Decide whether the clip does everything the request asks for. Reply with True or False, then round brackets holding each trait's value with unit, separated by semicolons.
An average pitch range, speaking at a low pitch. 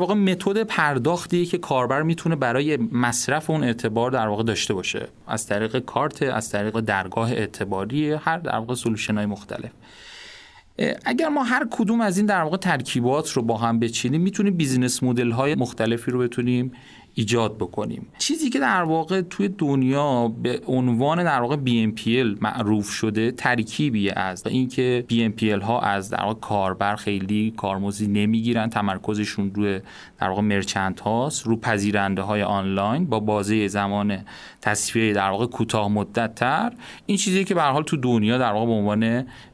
False (6.1 semitones; 120 Hz)